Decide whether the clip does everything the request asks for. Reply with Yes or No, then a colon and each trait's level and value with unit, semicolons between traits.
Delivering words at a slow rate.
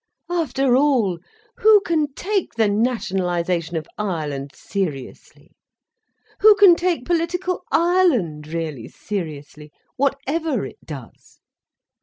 Yes: slow, 100 wpm